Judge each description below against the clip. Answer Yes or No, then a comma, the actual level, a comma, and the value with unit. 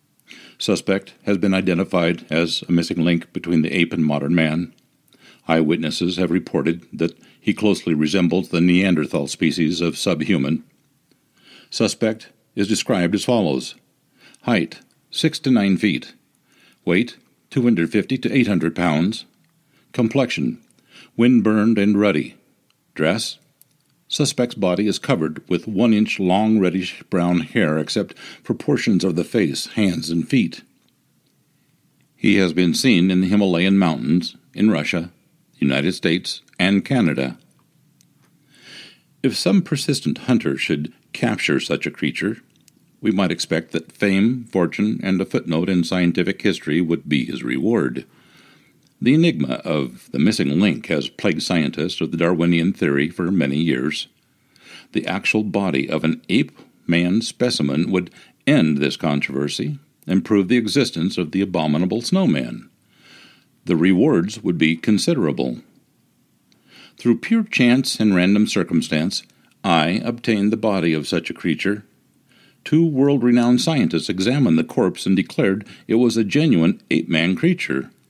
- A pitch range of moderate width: No, wide, 6.0 semitones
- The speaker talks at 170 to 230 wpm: No, slow, 135 wpm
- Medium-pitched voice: No, very low, 95 Hz